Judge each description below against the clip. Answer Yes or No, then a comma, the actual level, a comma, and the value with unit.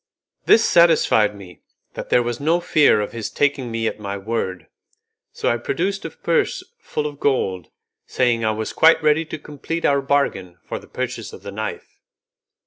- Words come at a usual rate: Yes, average, 180 wpm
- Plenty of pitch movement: Yes, wide, 6.1 semitones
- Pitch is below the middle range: Yes, low, 125 Hz